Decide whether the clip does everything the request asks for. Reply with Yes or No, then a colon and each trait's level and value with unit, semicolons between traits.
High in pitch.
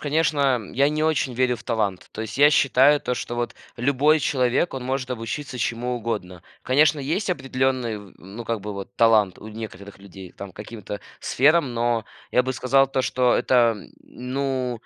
No: low, 125 Hz